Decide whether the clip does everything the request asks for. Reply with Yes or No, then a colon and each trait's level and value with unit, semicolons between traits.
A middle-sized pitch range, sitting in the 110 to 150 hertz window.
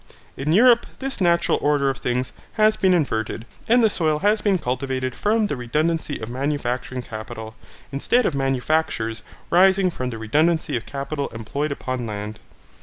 No: wide, 6.2 semitones; medium, 140 Hz